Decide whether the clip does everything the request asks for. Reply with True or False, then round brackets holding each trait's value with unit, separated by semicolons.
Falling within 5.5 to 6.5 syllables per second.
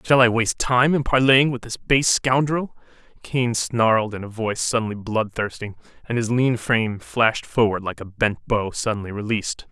False (5.1 syllables/s)